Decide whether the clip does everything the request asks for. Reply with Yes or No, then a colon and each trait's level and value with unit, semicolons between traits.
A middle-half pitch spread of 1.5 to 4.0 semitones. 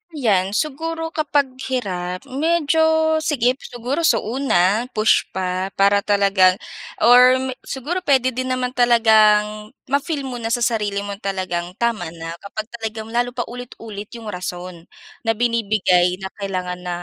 No: average, 4.8 semitones